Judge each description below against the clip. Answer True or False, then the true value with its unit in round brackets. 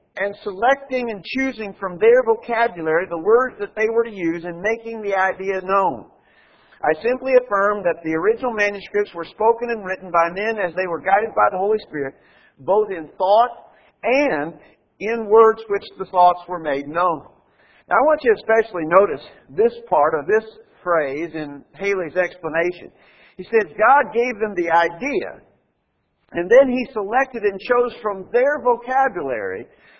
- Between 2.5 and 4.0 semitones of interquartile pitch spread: False (5.4 semitones)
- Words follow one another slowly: False (165 wpm)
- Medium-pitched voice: False (210 Hz)